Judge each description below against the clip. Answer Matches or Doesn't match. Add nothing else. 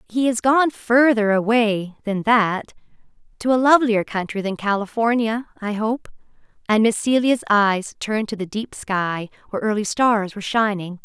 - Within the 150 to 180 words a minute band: Matches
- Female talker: Matches